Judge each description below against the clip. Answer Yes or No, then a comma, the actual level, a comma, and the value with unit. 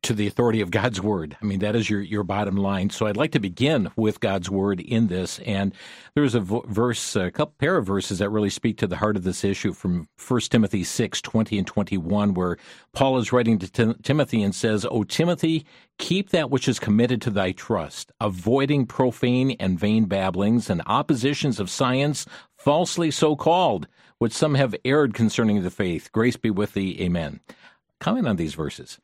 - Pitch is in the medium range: No, low, 110 Hz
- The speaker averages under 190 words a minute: No, fast, 205 wpm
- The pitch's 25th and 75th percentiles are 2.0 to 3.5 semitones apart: No, average, 4.3 semitones